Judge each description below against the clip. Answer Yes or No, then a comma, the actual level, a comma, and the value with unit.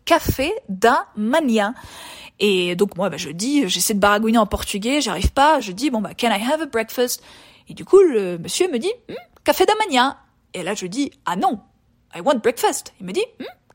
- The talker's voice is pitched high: Yes, high, 235 Hz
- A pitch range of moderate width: No, wide, 6.8 semitones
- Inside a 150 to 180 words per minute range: No, average, 205 wpm